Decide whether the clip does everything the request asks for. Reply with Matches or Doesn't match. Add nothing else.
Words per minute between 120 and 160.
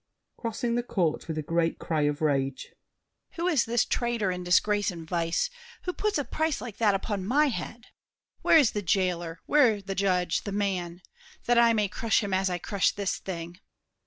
Doesn't match